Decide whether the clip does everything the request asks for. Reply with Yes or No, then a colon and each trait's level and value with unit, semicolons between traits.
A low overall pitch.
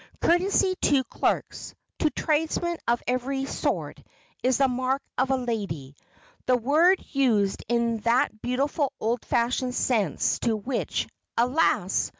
No: very high, 255 Hz